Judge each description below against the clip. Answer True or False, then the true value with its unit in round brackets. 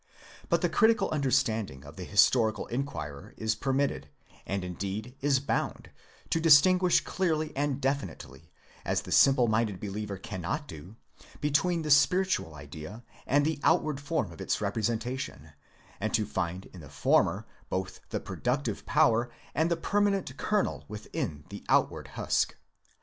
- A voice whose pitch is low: True (120 Hz)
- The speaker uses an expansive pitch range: True (7.5 semitones)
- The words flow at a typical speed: True (150 wpm)